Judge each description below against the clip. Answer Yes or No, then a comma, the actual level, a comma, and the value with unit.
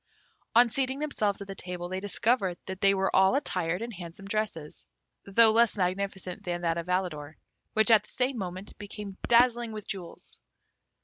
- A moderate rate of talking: Yes, average, 175 wpm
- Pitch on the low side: No, high, 195 Hz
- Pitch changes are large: No, average, 3.6 semitones